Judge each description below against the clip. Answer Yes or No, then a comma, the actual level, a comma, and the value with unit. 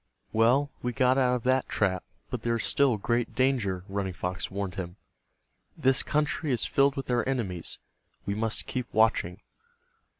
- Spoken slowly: No, average, 165 wpm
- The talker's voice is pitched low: Yes, low, 120 Hz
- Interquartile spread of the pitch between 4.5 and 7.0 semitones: Yes, average, 5.0 semitones